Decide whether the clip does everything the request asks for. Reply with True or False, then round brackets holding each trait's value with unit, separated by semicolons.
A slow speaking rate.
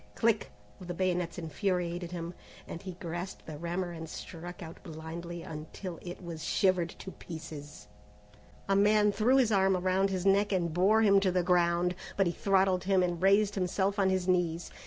False (180 wpm)